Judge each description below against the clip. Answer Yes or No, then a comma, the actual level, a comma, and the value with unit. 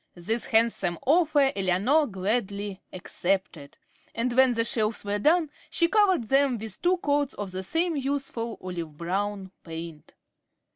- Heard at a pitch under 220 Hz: No, high, 225 Hz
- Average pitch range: No, wide, 7.0 semitones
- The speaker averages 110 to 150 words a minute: Yes, average, 140 wpm